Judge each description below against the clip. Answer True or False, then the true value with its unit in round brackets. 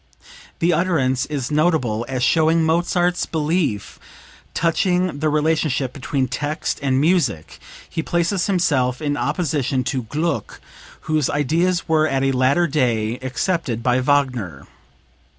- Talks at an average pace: False (125 wpm)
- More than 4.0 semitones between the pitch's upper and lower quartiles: True (4.4 semitones)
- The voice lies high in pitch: False (150 Hz)